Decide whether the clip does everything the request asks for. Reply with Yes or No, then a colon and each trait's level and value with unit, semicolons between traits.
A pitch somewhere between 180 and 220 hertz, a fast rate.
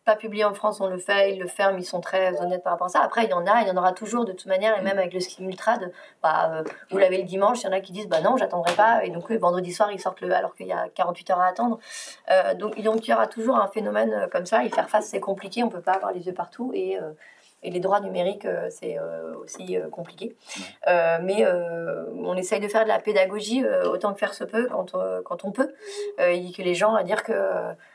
Yes: high, 190 Hz; fast, 270 wpm